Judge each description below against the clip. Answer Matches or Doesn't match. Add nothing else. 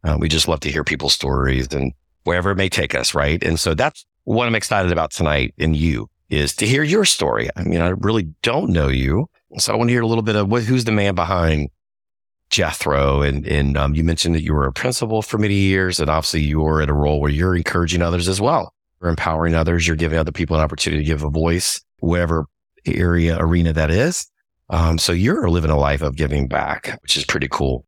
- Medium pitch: Doesn't match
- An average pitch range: Matches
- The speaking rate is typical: Doesn't match